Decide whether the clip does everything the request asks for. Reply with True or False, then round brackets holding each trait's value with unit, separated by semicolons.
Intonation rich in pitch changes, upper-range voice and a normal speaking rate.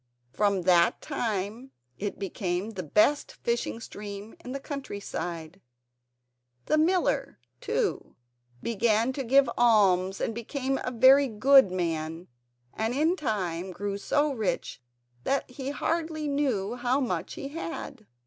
False (5.8 semitones; 230 Hz; 130 wpm)